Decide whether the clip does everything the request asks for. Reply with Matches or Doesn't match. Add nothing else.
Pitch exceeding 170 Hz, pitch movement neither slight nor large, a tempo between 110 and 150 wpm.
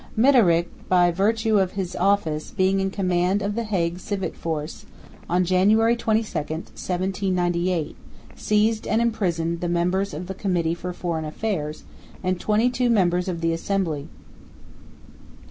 Matches